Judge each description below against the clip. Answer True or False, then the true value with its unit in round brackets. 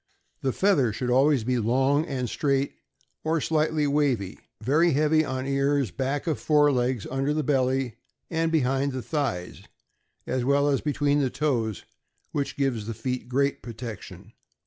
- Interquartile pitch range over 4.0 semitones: False (2.8 semitones)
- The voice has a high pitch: False (135 Hz)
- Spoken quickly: False (155 wpm)